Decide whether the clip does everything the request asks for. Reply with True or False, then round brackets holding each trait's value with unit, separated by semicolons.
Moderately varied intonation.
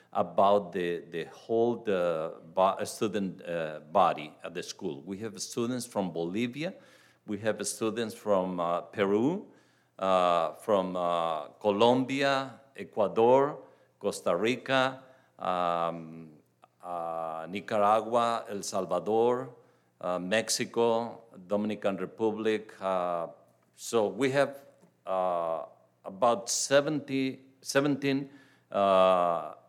False (6.0 semitones)